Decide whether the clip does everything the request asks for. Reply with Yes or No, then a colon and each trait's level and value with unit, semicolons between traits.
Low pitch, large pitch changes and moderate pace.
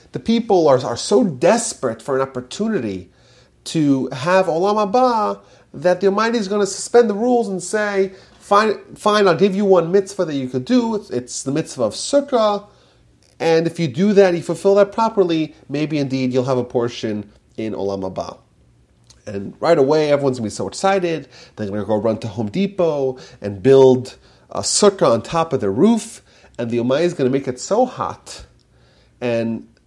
No: medium, 155 Hz; wide, 8.3 semitones; average, 185 wpm